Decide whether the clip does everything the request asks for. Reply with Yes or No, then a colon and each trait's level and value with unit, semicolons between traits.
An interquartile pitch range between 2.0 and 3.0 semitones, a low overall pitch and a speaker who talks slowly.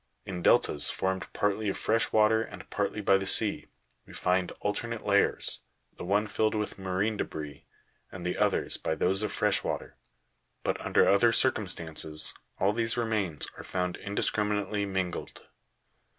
No: narrow, 2.6 semitones; low, 100 Hz; average, 150 wpm